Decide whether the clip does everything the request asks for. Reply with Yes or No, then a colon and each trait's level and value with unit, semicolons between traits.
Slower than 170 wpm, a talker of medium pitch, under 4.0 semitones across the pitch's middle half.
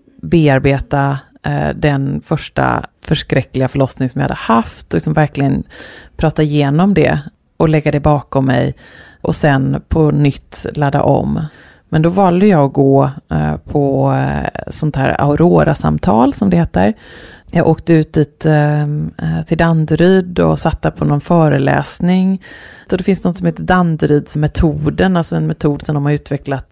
Yes: average, 140 wpm; medium, 150 Hz; average, 3.2 semitones